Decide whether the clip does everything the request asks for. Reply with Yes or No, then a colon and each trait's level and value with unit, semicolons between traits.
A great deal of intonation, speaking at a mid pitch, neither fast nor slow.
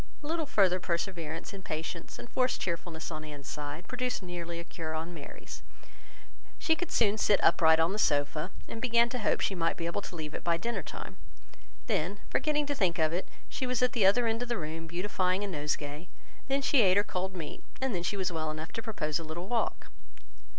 No: wide, 5.8 semitones; medium, 180 Hz; fast, 220 wpm